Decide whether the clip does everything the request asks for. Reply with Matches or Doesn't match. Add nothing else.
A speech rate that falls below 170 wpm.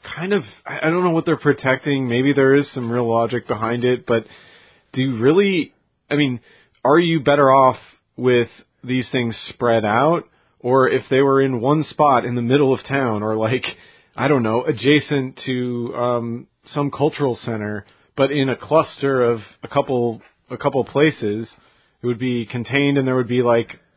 Doesn't match